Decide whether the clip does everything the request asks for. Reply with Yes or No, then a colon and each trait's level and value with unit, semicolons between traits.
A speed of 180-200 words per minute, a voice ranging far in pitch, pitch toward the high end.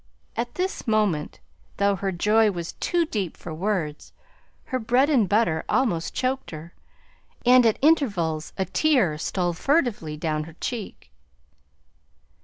No: slow, 135 wpm; wide, 7.0 semitones; high, 200 Hz